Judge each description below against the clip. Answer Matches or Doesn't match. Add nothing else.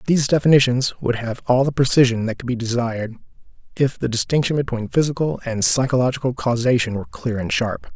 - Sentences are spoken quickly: Doesn't match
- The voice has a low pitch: Matches